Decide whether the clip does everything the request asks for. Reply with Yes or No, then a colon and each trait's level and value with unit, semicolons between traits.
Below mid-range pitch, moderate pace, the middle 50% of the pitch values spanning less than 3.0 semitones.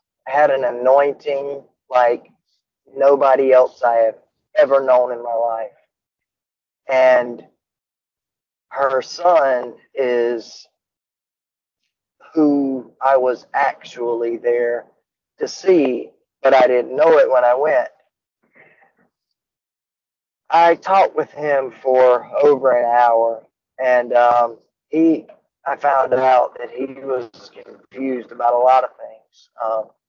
No: low, 130 Hz; slow, 110 wpm; narrow, 2.5 semitones